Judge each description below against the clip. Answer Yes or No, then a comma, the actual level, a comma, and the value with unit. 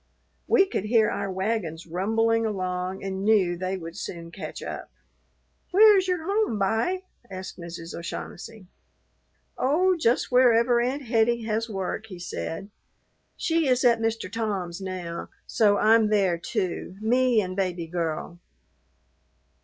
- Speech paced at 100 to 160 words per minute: Yes, average, 140 wpm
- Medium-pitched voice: No, high, 215 Hz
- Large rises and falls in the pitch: No, average, 4.5 semitones